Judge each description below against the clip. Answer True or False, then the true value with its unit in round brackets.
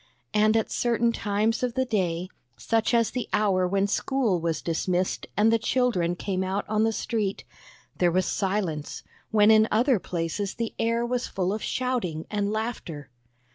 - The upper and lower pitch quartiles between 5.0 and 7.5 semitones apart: False (3.8 semitones)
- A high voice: True (210 Hz)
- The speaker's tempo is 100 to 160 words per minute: False (170 wpm)